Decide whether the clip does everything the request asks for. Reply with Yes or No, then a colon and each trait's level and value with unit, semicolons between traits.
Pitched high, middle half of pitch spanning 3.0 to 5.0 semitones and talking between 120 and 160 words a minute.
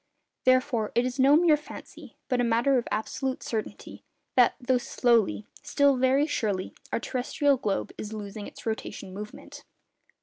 Yes: high, 245 Hz; average, 3.6 semitones; average, 155 wpm